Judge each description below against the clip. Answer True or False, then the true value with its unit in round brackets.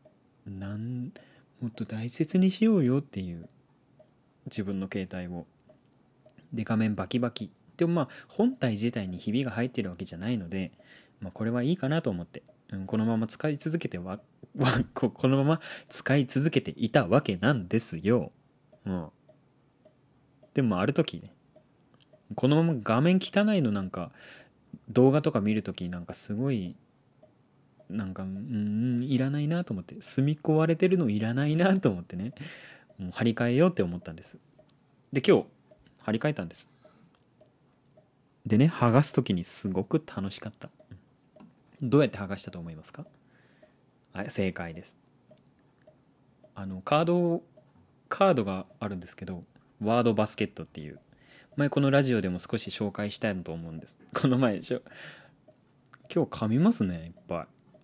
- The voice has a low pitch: True (120 Hz)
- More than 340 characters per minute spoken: False (300 characters per minute)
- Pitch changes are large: True (6.6 semitones)